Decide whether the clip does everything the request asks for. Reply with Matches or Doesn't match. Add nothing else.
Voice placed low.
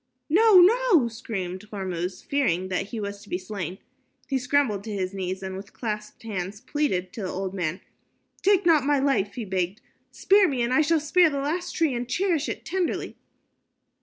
Doesn't match